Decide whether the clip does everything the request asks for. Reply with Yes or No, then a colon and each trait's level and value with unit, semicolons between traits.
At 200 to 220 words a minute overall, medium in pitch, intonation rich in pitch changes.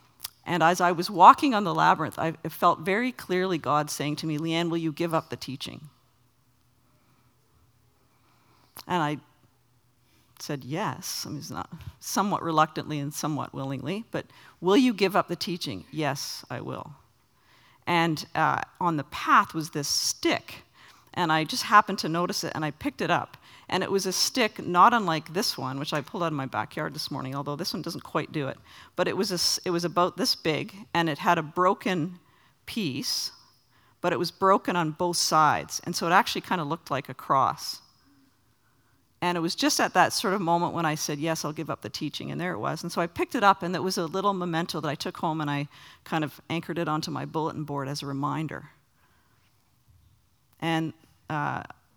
No: fast, 205 wpm; medium, 160 Hz; average, 3.9 semitones